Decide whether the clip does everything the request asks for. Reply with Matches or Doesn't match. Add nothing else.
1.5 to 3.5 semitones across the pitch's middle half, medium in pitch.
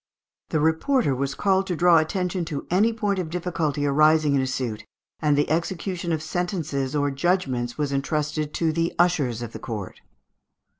Doesn't match